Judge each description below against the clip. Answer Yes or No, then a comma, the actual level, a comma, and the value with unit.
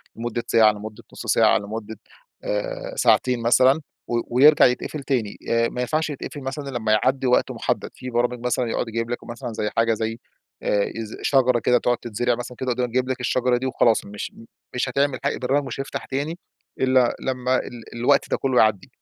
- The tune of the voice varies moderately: No, narrow, 2.2 semitones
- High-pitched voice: No, low, 125 Hz